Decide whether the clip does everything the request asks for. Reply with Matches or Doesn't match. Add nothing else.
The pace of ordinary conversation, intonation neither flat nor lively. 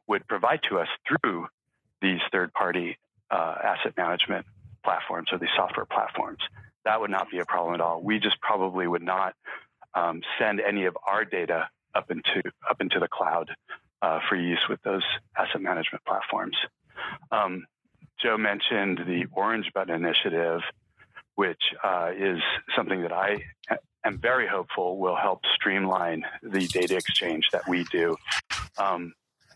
Doesn't match